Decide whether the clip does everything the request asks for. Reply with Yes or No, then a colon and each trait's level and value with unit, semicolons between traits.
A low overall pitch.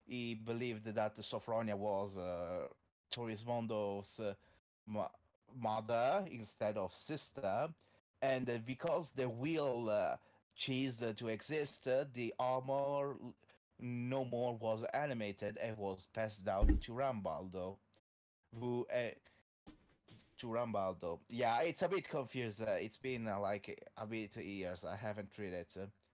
Yes: low, 110 Hz